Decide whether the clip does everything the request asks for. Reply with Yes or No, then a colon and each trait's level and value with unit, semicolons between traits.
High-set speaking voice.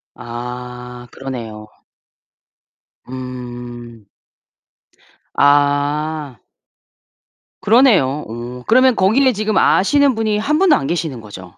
No: low, 135 Hz